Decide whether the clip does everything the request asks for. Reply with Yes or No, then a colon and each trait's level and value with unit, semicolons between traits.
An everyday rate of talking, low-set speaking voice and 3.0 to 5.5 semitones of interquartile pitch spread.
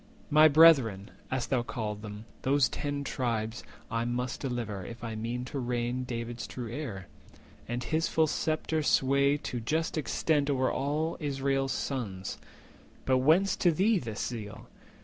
Yes: average, 150 wpm; low, 130 Hz; average, 3.8 semitones